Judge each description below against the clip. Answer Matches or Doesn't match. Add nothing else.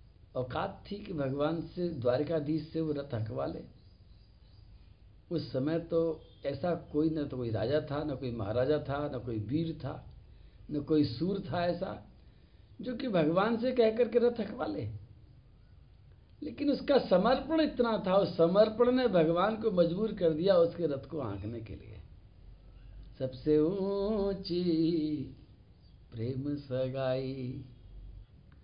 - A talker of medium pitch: Matches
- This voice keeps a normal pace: Matches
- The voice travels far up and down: Matches